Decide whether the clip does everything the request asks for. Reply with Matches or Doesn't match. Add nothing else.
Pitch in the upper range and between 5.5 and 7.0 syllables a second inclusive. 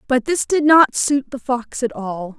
Doesn't match